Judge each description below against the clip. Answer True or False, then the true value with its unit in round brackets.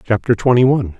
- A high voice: False (115 Hz)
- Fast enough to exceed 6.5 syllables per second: True (7.2 syllables/s)